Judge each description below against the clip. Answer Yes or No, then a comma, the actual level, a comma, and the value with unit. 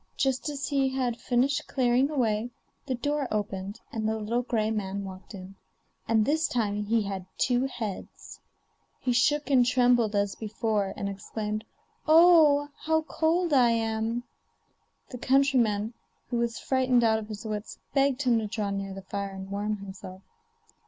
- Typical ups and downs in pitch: Yes, average, 4.1 semitones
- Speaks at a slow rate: No, average, 160 wpm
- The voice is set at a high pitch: Yes, high, 230 Hz